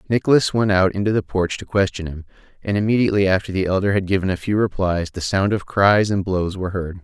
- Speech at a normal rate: No, fast, 230 wpm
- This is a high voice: No, very low, 95 Hz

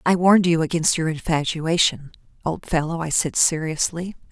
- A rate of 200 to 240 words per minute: No, average, 155 wpm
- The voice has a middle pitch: Yes, medium, 165 Hz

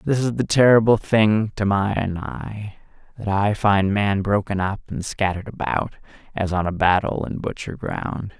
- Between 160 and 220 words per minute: Yes, average, 170 wpm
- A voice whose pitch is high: No, low, 105 Hz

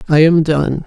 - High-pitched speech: No, medium, 155 Hz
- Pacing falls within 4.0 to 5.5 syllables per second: Yes, 4.4 syllables/s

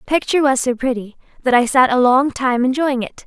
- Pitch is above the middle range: Yes, very high, 260 Hz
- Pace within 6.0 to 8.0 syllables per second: Yes, 6.1 syllables/s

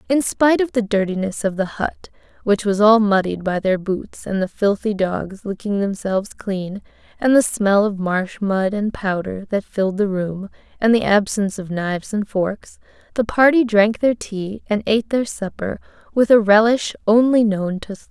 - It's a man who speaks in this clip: No, female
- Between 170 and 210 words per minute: Yes, average, 190 wpm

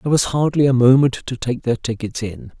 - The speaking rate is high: Yes, fast, 230 wpm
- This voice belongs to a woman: No, male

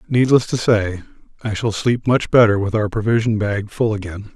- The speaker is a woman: No, male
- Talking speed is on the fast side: No, average, 195 wpm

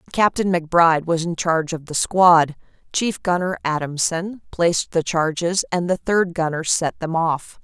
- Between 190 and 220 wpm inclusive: No, average, 165 wpm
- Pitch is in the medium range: Yes, medium, 170 Hz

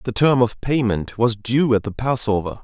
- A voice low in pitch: Yes, low, 115 Hz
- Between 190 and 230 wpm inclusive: Yes, fast, 205 wpm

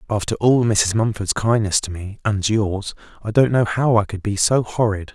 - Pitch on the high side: No, low, 105 Hz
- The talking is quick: Yes, fast, 210 wpm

